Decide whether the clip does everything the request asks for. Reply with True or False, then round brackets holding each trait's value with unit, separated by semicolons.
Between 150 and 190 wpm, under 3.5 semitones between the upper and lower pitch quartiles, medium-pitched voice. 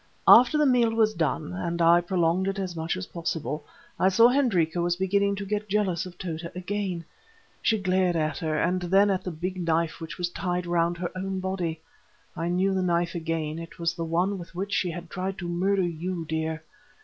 False (200 wpm; 2.4 semitones; 175 Hz)